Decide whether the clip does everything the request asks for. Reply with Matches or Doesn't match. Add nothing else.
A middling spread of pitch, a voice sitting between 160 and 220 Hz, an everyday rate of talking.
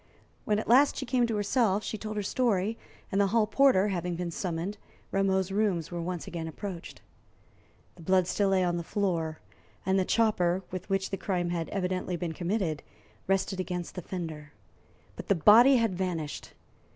Matches